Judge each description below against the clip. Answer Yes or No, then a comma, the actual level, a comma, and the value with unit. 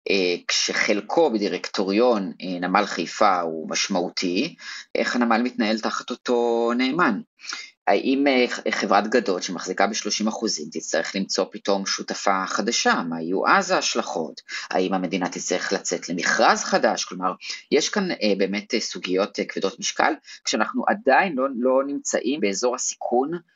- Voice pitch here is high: No, low, 105 Hz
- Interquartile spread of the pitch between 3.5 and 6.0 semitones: Yes, average, 4.4 semitones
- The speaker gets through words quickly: No, average, 130 wpm